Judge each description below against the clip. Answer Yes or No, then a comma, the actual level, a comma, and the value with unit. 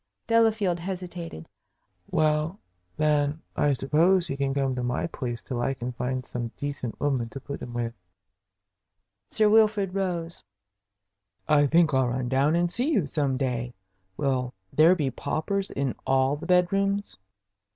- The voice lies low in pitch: No, medium, 145 Hz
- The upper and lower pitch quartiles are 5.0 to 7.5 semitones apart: Yes, wide, 5.4 semitones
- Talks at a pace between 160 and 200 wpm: No, average, 150 wpm